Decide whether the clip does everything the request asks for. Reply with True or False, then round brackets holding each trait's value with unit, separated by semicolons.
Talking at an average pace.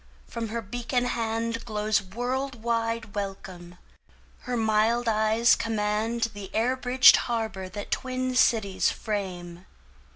False (105 wpm)